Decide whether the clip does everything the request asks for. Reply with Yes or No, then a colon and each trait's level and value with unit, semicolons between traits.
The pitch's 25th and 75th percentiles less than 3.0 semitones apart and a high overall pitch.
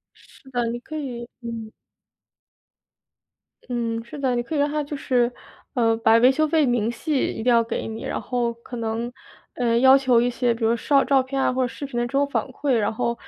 Yes: narrow, 2.6 semitones; high, 245 Hz